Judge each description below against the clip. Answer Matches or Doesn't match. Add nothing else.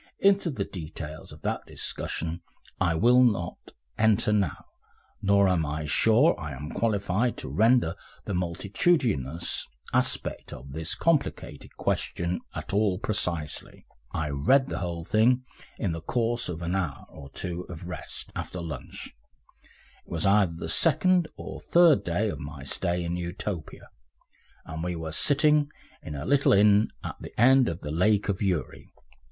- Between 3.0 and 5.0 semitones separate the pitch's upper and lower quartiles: Doesn't match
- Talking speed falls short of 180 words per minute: Matches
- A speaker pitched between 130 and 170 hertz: Doesn't match